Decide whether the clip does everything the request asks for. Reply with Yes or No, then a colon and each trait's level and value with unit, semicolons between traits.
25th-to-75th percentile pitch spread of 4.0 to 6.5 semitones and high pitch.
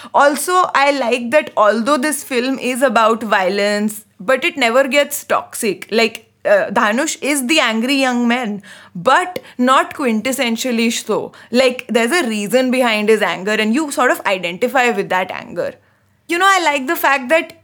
Yes: average, 4.3 semitones; very high, 250 Hz